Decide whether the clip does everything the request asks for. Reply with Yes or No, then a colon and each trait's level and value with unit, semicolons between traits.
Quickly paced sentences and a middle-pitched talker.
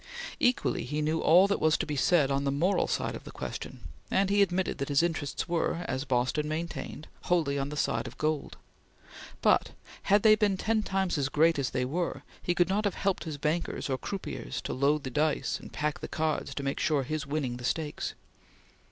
Yes: fast, 215 wpm; medium, 155 Hz